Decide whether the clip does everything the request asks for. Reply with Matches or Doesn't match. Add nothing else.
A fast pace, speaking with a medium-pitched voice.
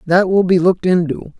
Matches